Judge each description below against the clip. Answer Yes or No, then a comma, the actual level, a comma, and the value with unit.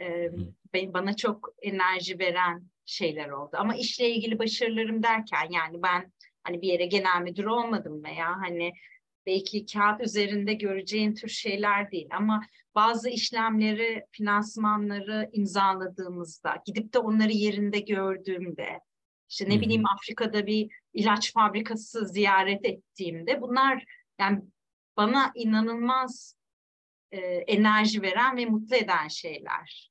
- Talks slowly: No, average, 120 wpm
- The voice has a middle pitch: No, high, 205 Hz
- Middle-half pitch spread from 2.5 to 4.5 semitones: Yes, average, 3.1 semitones